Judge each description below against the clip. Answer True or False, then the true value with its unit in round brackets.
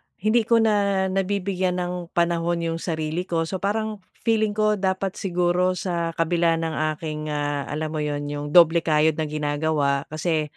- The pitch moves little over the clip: False (3.5 semitones)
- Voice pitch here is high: False (170 Hz)